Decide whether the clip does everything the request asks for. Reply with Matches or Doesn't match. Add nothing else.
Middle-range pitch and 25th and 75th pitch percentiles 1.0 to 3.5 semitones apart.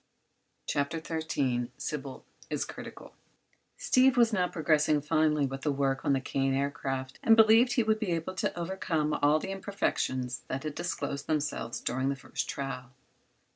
Doesn't match